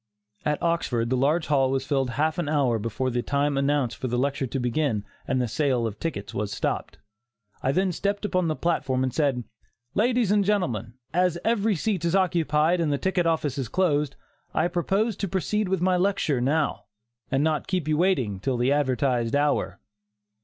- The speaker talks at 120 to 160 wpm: No, average, 190 wpm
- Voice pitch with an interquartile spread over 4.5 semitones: Yes, wide, 5.6 semitones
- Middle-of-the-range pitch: Yes, medium, 145 Hz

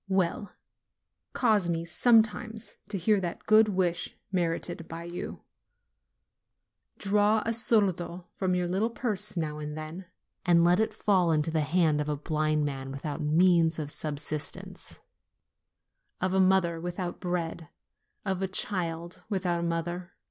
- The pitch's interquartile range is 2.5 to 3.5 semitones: Yes, average, 2.8 semitones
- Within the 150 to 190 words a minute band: No, average, 140 wpm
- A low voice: No, medium, 175 Hz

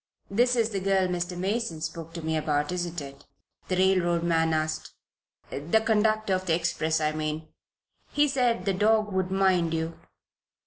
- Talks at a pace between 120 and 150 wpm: No, average, 170 wpm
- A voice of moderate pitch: Yes, medium, 180 Hz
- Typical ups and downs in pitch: Yes, average, 3.8 semitones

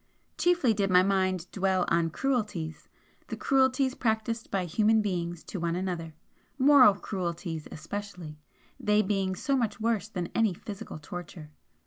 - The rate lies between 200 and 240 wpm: No, average, 140 wpm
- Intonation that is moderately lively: Yes, average, 4.3 semitones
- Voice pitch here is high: Yes, high, 195 Hz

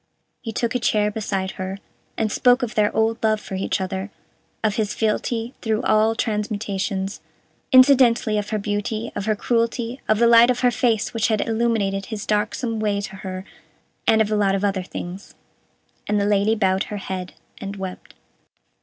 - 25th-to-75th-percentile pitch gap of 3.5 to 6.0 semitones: No, narrow, 2.4 semitones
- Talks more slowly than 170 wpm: No, average, 180 wpm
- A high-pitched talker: Yes, high, 215 Hz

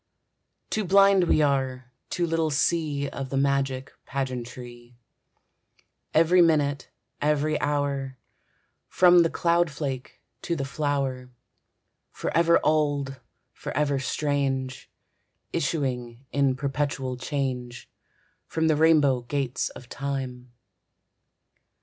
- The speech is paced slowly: Yes, slow, 95 wpm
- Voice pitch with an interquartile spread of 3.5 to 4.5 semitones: No, average, 2.9 semitones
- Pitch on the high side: No, medium, 140 Hz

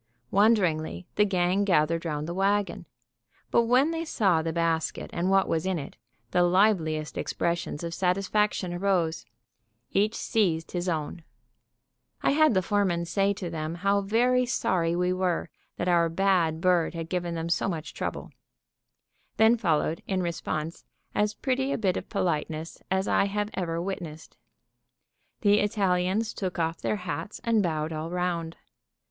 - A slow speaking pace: No, average, 155 wpm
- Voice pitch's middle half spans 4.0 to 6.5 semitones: No, average, 3.4 semitones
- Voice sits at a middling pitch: Yes, medium, 180 Hz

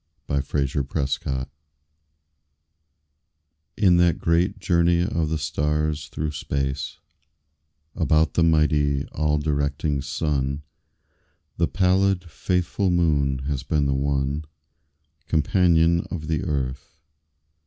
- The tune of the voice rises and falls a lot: No, average, 3.3 semitones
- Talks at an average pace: No, slow, 100 wpm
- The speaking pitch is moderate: No, very low, 75 Hz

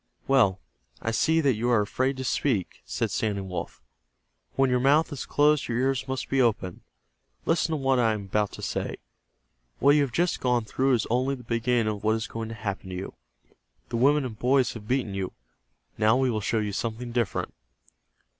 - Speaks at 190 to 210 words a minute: Yes, average, 200 wpm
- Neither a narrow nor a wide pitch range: Yes, average, 3.7 semitones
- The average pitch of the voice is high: No, low, 120 Hz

